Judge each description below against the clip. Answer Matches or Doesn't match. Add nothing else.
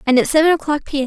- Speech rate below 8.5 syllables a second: Doesn't match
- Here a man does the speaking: Doesn't match